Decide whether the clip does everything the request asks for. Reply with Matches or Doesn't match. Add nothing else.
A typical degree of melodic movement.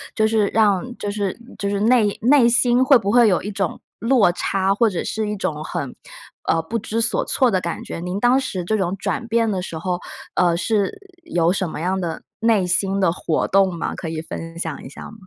Matches